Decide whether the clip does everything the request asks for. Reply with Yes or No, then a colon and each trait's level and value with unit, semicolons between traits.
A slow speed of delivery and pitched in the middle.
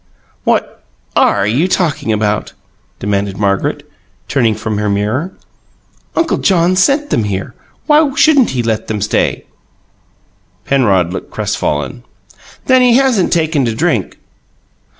No: slow, 125 wpm; low, 115 Hz